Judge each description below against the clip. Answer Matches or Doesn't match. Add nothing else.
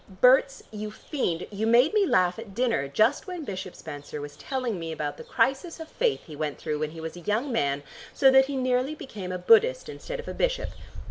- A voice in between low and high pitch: Doesn't match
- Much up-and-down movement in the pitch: Matches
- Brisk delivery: Matches